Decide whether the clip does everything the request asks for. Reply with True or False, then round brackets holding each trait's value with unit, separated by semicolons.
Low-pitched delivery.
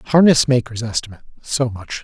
True (125 Hz)